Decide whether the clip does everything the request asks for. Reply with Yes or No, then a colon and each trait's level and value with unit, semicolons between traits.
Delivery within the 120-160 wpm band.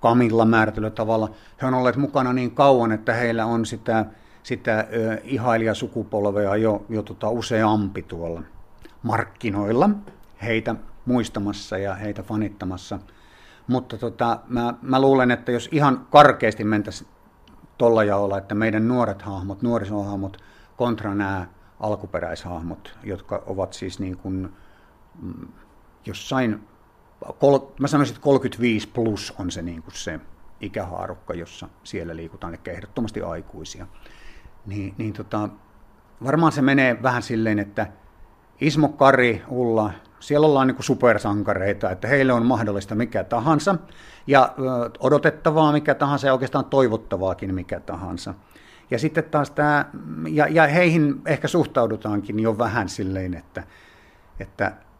Yes: average, 125 wpm